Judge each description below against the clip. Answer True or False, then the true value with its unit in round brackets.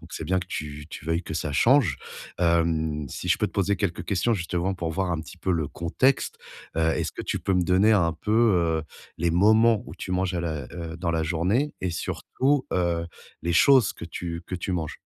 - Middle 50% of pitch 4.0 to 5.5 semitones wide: False (2.9 semitones)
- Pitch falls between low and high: False (85 Hz)